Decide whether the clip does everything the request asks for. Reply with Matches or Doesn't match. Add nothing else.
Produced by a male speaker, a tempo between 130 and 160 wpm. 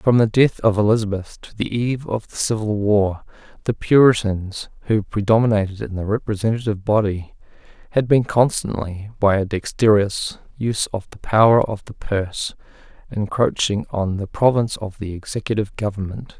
Matches